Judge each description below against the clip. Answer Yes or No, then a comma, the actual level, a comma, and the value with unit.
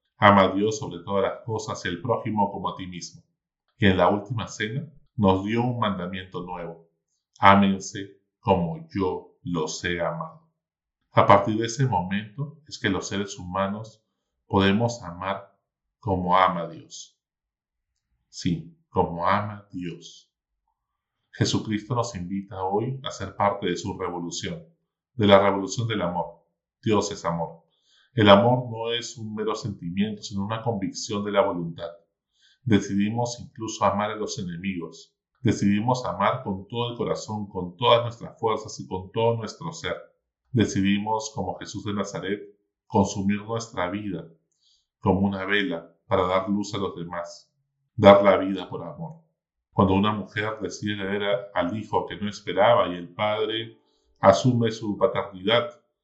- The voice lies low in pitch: Yes, low, 100 Hz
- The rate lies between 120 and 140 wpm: No, average, 150 wpm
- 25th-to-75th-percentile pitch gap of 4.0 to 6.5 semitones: No, average, 3.2 semitones